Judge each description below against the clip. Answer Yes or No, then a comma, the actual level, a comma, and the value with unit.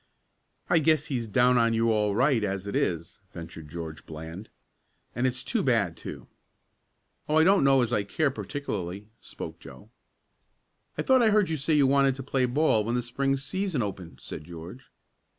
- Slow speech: No, average, 185 wpm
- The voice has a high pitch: No, low, 120 Hz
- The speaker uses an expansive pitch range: Yes, wide, 6.1 semitones